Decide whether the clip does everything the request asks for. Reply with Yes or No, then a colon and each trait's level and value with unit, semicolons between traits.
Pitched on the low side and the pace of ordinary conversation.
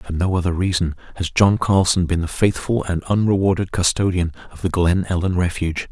Yes: very low, 90 Hz; average, 185 wpm